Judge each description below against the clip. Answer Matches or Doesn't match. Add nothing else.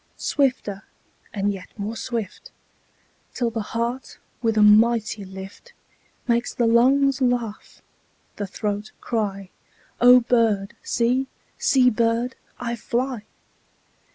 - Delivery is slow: Matches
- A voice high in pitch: Matches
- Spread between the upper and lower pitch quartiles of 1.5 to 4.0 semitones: Matches